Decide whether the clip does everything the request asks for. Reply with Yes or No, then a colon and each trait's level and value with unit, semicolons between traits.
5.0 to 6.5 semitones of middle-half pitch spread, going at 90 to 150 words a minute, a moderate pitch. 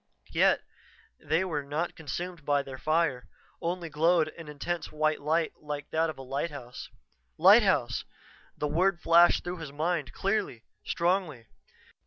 No: average, 3.1 semitones; average, 140 wpm; medium, 155 Hz